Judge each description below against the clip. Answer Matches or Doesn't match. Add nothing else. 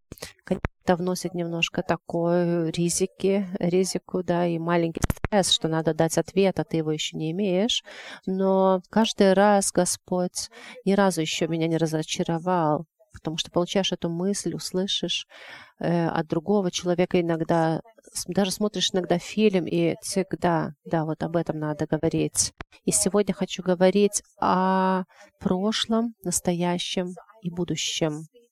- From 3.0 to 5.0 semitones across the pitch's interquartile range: Doesn't match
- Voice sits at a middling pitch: Matches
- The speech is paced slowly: Matches